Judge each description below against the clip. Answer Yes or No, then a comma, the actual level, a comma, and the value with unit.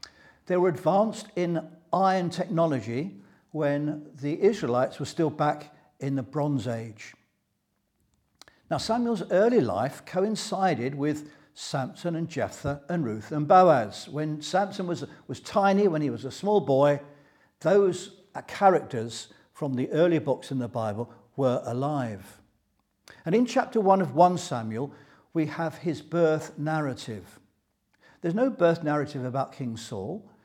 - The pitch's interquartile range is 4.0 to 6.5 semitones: Yes, wide, 5.5 semitones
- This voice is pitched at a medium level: Yes, medium, 150 Hz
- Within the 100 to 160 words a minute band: Yes, average, 140 wpm